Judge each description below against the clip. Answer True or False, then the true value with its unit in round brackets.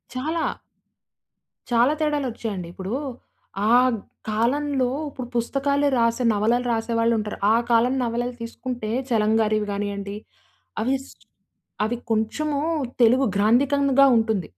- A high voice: True (235 Hz)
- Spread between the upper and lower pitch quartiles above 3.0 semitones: True (3.4 semitones)